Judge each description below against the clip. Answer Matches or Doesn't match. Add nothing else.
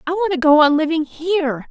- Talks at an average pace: Doesn't match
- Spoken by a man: Doesn't match